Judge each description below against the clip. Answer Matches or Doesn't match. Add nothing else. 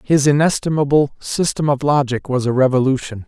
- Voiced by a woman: Doesn't match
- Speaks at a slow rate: Doesn't match